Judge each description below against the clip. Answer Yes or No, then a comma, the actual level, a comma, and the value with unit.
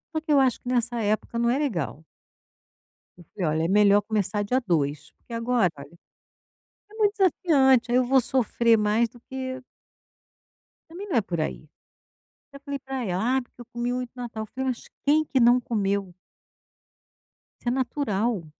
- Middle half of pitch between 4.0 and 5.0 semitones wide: Yes, average, 4.3 semitones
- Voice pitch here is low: No, high, 240 Hz